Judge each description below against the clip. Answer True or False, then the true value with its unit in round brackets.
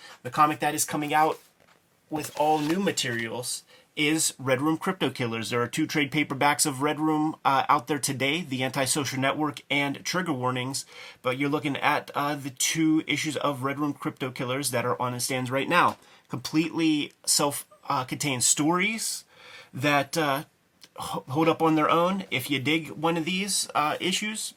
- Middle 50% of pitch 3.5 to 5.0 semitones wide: False (2.7 semitones)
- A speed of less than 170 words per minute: False (180 wpm)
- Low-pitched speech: False (150 Hz)